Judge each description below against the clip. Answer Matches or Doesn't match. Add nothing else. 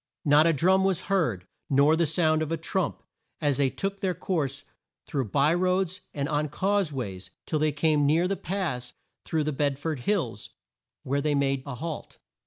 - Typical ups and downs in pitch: Matches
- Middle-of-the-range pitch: Matches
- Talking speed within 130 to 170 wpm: Doesn't match